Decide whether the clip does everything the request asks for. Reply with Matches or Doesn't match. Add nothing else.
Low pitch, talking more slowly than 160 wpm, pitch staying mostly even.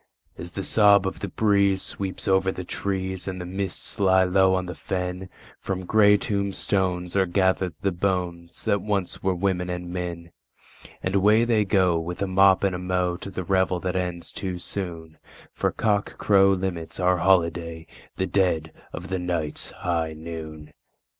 Doesn't match